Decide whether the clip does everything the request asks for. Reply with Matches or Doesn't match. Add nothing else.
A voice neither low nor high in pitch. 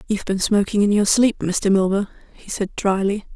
Doesn't match